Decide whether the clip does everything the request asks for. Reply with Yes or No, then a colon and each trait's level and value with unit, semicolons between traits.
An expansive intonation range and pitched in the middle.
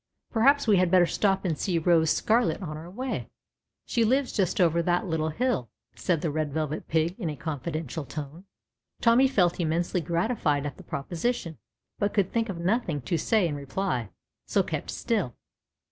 No: average, 4.7 semitones; medium, 175 Hz